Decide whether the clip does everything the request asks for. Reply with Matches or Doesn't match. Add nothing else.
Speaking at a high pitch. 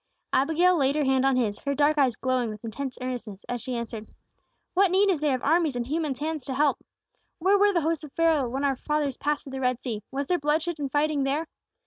Matches